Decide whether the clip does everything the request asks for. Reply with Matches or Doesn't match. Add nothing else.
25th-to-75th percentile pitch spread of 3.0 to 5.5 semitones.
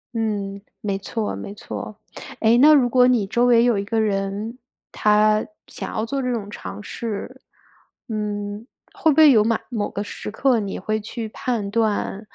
Doesn't match